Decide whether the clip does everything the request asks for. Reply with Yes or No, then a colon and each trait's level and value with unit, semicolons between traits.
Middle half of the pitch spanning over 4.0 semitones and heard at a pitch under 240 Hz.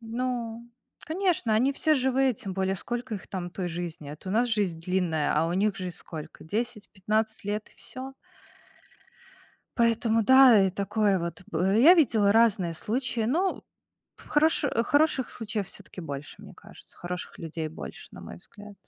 Yes: average, 5.1 semitones; high, 215 Hz